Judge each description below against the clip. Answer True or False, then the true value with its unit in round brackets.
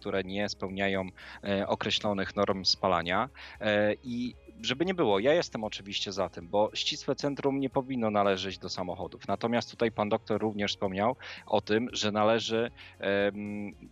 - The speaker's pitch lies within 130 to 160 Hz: False (105 Hz)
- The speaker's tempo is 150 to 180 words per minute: True (160 wpm)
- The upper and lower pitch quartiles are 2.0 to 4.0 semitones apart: True (2.8 semitones)